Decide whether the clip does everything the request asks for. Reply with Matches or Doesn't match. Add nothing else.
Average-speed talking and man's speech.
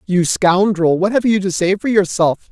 Doesn't match